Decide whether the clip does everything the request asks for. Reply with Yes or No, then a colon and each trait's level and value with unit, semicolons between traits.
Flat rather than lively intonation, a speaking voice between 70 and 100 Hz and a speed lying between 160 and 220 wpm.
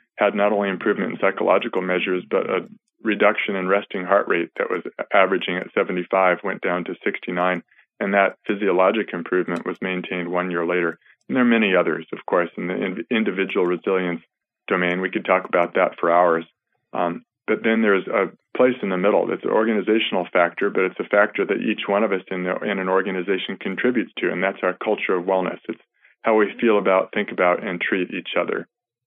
Yes: narrow, 1.4 semitones; very low, 90 Hz; average, 200 wpm